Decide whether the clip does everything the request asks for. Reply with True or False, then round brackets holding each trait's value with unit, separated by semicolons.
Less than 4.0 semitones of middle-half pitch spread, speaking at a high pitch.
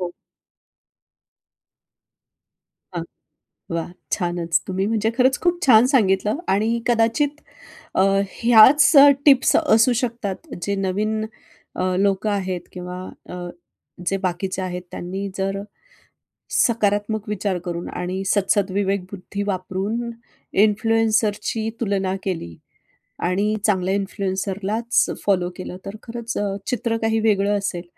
True (3.0 semitones; 200 Hz)